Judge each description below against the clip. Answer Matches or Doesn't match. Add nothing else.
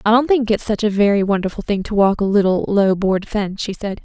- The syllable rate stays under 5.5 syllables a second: Doesn't match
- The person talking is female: Matches